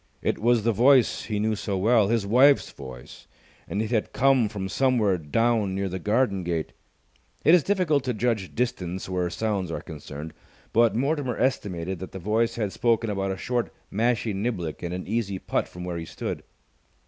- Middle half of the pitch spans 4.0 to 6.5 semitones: Yes, average, 4.3 semitones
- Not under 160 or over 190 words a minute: Yes, average, 185 wpm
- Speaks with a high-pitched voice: No, low, 105 Hz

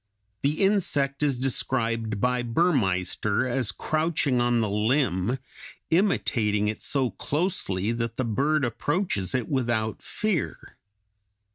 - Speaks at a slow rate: Yes, slow, 115 wpm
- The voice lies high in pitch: No, low, 125 Hz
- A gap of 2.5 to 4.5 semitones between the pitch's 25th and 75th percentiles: No, average, 5.1 semitones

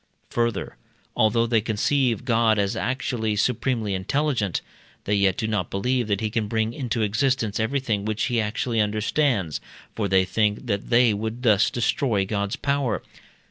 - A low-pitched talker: Yes, low, 110 Hz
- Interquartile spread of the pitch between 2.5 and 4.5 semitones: Yes, average, 2.9 semitones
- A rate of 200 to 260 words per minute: No, average, 155 wpm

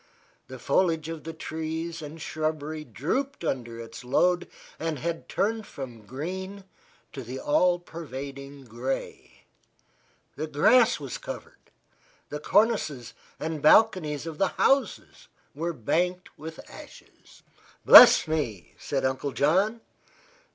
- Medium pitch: Yes, medium, 155 Hz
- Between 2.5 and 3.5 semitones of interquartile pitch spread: No, average, 4.4 semitones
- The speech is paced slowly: Yes, slow, 120 wpm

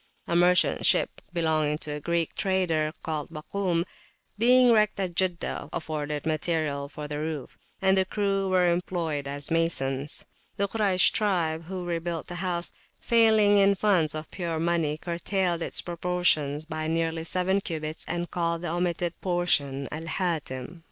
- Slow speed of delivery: No, average, 155 wpm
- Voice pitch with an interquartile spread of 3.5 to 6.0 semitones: No, average, 2.9 semitones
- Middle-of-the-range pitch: Yes, medium, 170 Hz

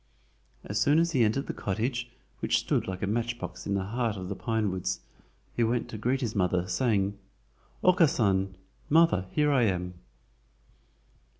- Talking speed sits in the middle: Yes, average, 165 wpm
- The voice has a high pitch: No, low, 110 Hz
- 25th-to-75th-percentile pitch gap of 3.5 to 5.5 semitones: Yes, average, 4.5 semitones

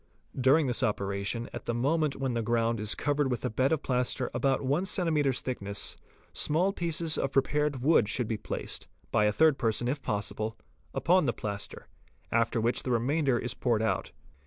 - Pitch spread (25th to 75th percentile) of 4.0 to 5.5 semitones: Yes, average, 4.3 semitones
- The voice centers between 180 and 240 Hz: No, low, 125 Hz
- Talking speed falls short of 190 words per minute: No, average, 195 wpm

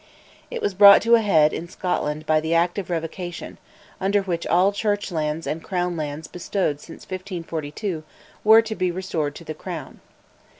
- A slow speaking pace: No, average, 175 wpm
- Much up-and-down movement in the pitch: No, average, 3.7 semitones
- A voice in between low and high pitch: Yes, medium, 175 Hz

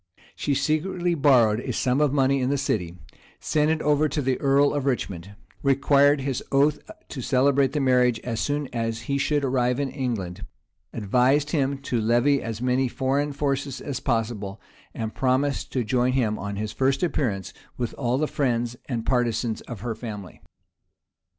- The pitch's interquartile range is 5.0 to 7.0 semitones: No, average, 3.2 semitones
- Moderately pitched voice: No, low, 130 Hz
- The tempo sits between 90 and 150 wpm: No, average, 170 wpm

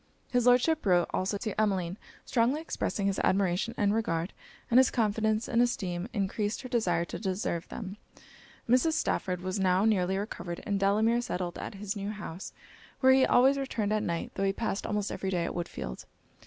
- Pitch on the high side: Yes, high, 205 Hz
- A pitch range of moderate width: Yes, average, 3.8 semitones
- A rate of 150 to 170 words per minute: No, average, 180 wpm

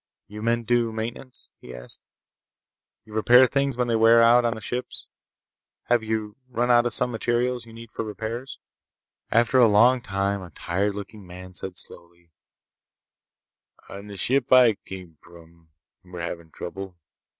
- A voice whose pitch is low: Yes, low, 110 Hz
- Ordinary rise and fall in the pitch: Yes, average, 4.1 semitones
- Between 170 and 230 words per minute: No, average, 160 wpm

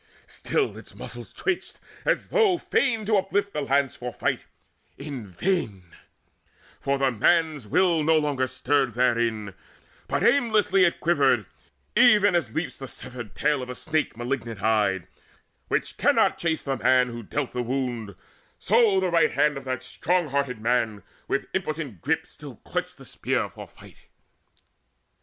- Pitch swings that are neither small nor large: No, wide, 6.3 semitones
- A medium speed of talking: Yes, average, 155 wpm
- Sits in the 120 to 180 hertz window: Yes, medium, 140 Hz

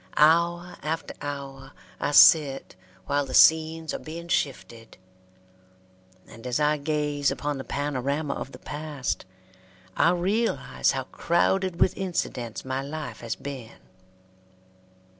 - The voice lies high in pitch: No, medium, 145 Hz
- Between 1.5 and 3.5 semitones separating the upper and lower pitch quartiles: Yes, average, 3.2 semitones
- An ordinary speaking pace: No, slow, 120 wpm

